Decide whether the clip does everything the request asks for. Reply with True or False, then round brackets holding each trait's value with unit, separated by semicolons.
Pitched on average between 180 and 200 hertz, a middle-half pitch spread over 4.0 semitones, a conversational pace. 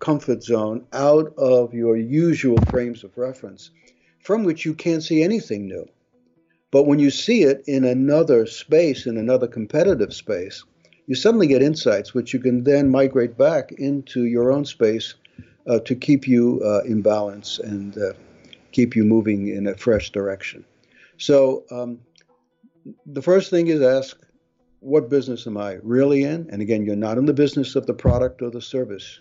False (125 Hz; 4.5 semitones; 175 wpm)